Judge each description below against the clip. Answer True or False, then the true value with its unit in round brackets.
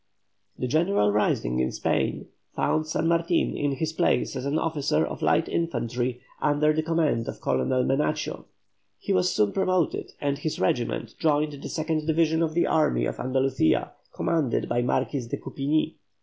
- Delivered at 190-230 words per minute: False (165 wpm)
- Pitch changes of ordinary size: True (4.6 semitones)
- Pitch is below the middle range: False (145 Hz)